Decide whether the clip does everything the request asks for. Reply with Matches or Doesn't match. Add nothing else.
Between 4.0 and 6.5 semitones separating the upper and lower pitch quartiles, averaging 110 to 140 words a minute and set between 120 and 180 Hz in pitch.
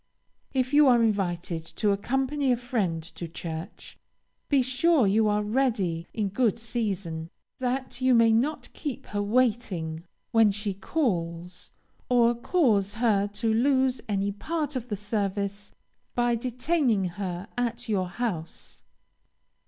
Doesn't match